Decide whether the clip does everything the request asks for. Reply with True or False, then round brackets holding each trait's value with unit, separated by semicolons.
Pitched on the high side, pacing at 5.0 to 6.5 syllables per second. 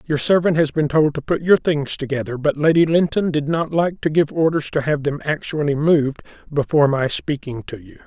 False (150 Hz; 5.4 syllables/s)